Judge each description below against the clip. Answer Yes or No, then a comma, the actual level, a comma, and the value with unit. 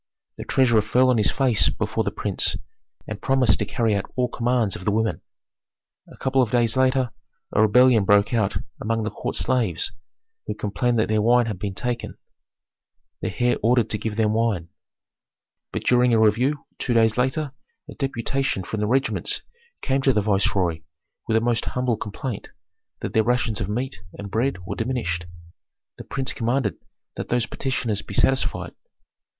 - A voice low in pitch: Yes, low, 115 Hz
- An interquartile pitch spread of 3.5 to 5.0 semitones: No, average, 3.1 semitones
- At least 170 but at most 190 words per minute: Yes, average, 175 wpm